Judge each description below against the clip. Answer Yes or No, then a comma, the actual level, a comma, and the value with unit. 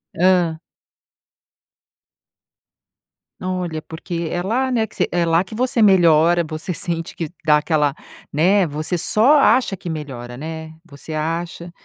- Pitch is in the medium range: Yes, medium, 170 Hz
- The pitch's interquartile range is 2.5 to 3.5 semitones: Yes, average, 2.8 semitones